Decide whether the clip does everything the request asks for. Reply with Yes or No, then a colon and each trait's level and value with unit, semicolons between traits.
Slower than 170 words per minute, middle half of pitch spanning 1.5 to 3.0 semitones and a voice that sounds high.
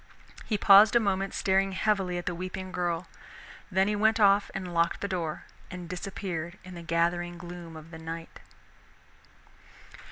No: average, 160 wpm; narrow, 2.4 semitones; medium, 180 Hz